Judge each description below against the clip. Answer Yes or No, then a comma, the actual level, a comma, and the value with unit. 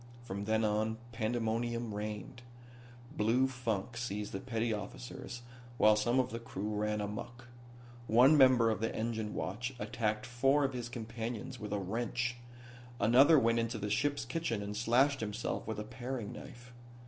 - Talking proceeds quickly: No, average, 160 wpm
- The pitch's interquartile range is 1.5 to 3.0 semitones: Yes, narrow, 2.6 semitones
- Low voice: Yes, low, 115 Hz